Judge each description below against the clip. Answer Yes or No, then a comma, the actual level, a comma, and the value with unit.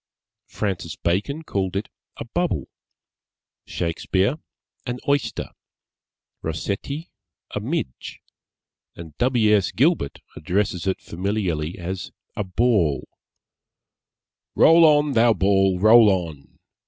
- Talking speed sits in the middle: No, slow, 100 wpm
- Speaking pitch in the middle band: No, low, 100 Hz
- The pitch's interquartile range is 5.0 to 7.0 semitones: Yes, wide, 5.5 semitones